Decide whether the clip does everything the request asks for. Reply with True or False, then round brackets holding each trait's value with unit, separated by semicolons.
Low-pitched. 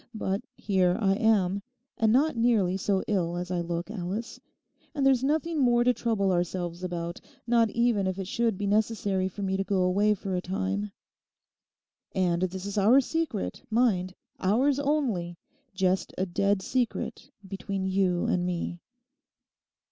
False (195 Hz)